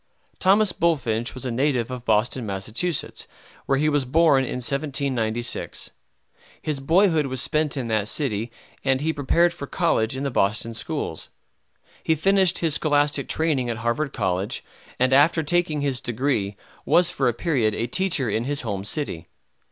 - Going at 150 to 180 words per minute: Yes, average, 160 wpm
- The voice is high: No, low, 135 Hz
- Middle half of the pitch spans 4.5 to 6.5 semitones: Yes, average, 4.9 semitones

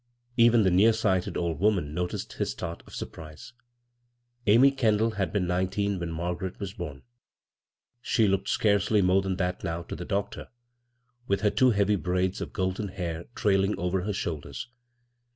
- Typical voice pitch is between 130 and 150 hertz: No, very low, 95 Hz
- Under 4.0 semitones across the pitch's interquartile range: Yes, average, 2.7 semitones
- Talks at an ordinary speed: Yes, average, 165 wpm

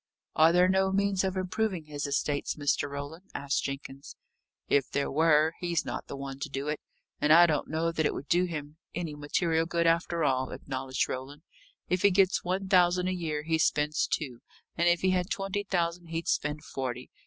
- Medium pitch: Yes, medium, 160 Hz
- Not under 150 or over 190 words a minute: No, average, 200 wpm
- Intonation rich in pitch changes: No, average, 3.7 semitones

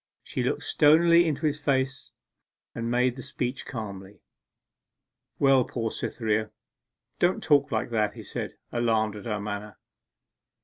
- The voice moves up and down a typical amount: Yes, average, 4.3 semitones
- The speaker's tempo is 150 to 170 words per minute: No, slow, 135 wpm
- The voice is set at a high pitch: No, low, 120 Hz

